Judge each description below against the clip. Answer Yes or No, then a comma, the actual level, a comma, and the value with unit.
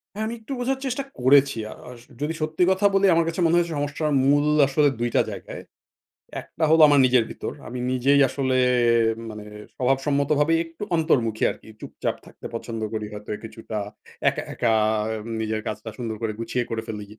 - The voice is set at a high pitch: No, medium, 140 Hz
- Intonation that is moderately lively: No, wide, 5.8 semitones